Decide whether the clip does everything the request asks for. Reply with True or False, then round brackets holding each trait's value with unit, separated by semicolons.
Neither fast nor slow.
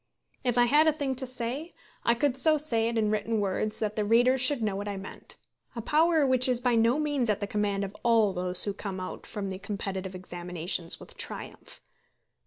False (215 wpm)